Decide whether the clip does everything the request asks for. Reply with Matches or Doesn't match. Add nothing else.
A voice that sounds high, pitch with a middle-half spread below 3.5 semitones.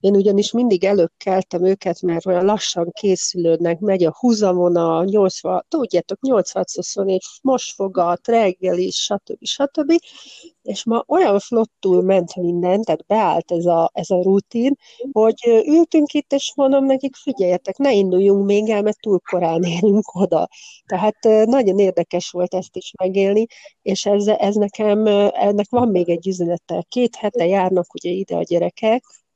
Doesn't match